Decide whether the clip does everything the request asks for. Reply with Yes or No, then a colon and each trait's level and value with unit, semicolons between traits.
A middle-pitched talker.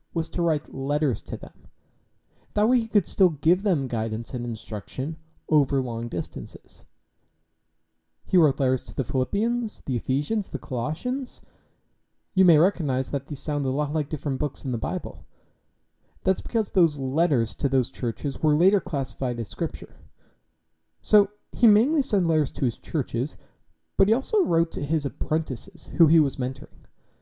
Yes: medium, 145 Hz